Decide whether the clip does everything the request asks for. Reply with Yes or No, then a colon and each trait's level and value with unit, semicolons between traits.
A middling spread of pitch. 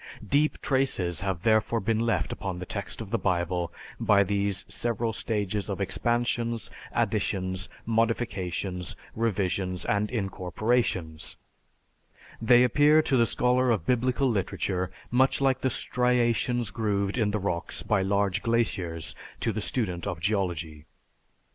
Yes: average, 4.2 semitones